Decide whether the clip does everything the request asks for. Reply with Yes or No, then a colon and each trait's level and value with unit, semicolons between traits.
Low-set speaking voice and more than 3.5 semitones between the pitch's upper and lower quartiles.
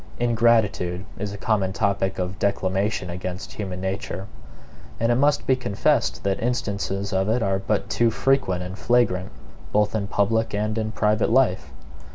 No: low, 100 Hz; average, 2.9 semitones